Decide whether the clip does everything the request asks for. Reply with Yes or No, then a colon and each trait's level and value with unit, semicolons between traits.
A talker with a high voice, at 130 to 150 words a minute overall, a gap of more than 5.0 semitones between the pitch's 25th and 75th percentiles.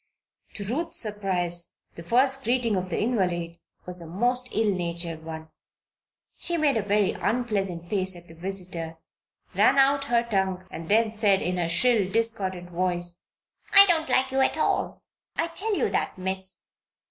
No: high, 195 Hz; average, 165 wpm; wide, 5.6 semitones